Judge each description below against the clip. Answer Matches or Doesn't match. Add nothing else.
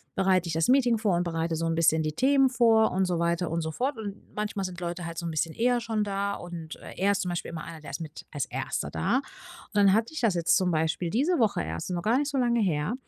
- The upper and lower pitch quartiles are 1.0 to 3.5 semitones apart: Doesn't match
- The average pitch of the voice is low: Doesn't match